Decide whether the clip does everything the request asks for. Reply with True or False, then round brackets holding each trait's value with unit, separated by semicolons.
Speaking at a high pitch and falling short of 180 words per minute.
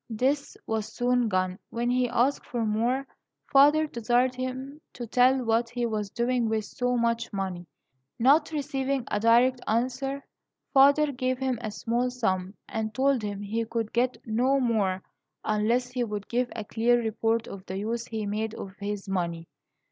True (235 Hz; 170 wpm)